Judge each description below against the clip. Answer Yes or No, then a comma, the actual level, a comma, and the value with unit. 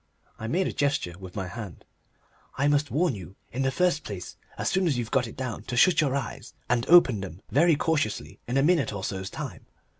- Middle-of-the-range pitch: No, low, 130 Hz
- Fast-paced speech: Yes, fast, 220 wpm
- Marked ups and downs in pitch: Yes, wide, 6.7 semitones